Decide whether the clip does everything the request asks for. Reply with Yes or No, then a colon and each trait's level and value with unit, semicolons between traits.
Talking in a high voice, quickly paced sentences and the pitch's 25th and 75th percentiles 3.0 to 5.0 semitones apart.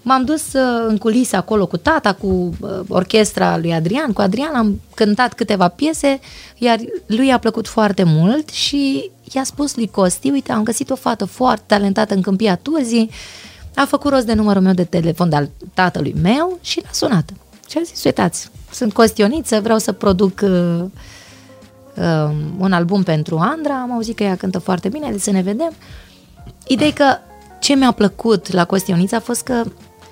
No: high, 215 Hz; fast, 175 wpm; wide, 5.4 semitones